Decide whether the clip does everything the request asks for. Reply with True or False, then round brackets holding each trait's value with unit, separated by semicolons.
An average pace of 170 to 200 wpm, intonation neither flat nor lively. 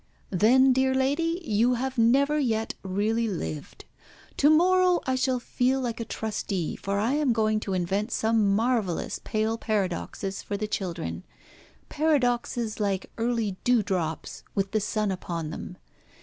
False (145 wpm; 4.6 semitones)